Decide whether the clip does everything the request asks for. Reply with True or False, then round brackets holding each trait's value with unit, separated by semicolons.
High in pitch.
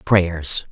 False (90 Hz)